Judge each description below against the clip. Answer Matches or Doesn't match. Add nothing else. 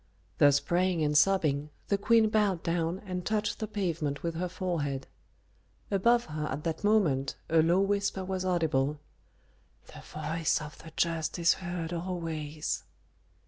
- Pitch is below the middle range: Doesn't match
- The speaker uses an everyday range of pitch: Matches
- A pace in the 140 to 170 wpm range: Matches